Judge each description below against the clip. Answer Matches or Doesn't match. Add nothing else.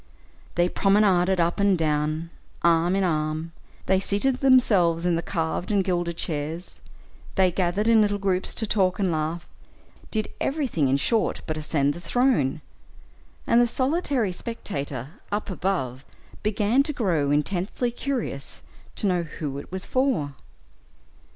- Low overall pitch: Doesn't match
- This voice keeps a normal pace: Matches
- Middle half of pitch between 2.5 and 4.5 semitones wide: Doesn't match